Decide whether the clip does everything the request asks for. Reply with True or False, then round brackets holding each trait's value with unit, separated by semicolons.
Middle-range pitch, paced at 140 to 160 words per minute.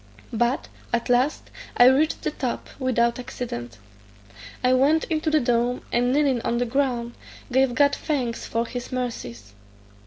False (245 Hz; 150 wpm)